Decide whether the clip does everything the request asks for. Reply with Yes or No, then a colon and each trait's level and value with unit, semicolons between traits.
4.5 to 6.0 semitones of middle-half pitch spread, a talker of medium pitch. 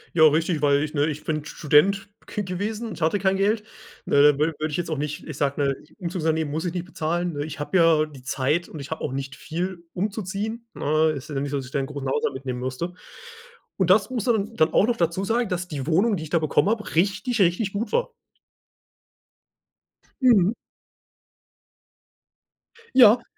Yes: average, 5.1 semitones; medium, 170 Hz